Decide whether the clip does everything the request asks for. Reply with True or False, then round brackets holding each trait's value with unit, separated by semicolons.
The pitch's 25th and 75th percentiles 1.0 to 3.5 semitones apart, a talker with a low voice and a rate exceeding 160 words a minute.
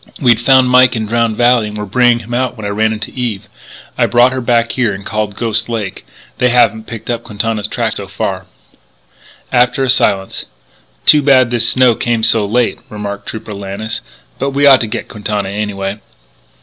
True (2.8 semitones; 115 Hz; 190 wpm)